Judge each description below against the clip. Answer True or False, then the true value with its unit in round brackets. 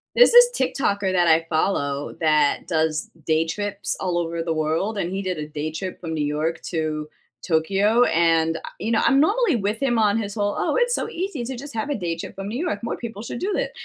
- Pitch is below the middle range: False (190 Hz)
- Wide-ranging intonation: True (6.0 semitones)